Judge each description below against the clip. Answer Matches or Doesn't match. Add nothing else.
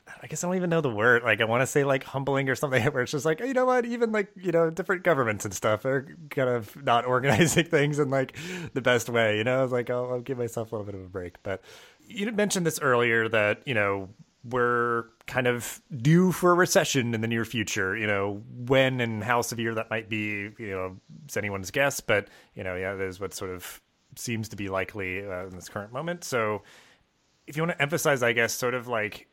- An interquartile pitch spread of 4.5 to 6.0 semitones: Matches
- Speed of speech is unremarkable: Doesn't match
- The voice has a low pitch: Matches